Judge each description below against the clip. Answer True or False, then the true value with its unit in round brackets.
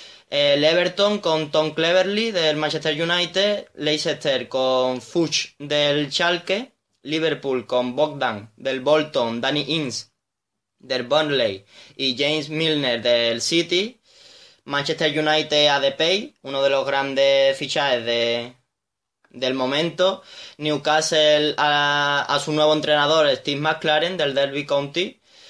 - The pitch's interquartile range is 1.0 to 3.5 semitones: True (2.9 semitones)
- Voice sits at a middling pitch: True (150 Hz)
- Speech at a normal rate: False (120 wpm)